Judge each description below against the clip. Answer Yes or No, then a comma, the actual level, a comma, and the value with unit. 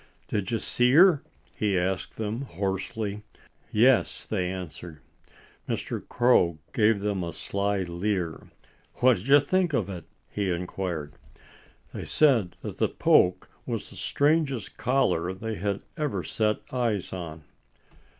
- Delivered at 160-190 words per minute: No, slow, 135 wpm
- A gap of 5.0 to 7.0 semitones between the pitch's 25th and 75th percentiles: Yes, average, 5.3 semitones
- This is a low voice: Yes, low, 100 Hz